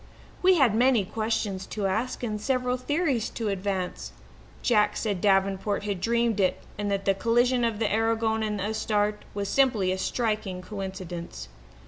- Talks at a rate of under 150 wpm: No, average, 160 wpm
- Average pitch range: Yes, average, 3.0 semitones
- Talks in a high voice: Yes, high, 210 Hz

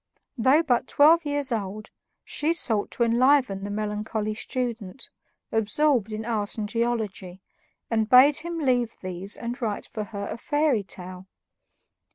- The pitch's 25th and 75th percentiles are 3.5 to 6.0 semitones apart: Yes, average, 4.2 semitones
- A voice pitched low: No, high, 230 Hz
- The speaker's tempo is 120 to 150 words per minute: Yes, average, 145 wpm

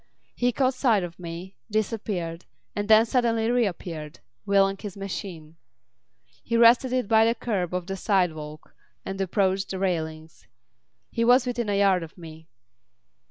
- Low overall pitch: No, high, 195 Hz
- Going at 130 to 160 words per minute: Yes, average, 150 wpm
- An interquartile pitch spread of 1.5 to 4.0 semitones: No, average, 4.8 semitones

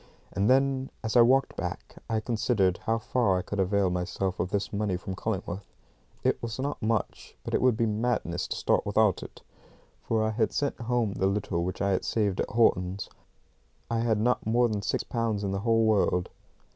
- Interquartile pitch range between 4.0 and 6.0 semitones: No, average, 3.2 semitones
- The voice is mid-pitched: No, low, 110 Hz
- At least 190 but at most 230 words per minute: Yes, average, 200 wpm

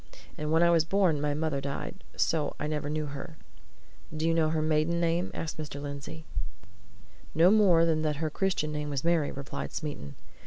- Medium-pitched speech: Yes, medium, 155 Hz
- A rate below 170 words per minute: No, average, 190 wpm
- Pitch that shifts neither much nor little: No, narrow, 2.0 semitones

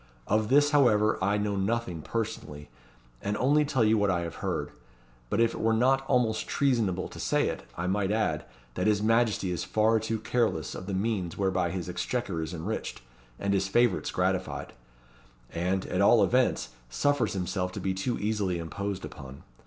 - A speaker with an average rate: Yes, average, 180 wpm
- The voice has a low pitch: Yes, low, 105 Hz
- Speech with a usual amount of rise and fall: Yes, average, 3.8 semitones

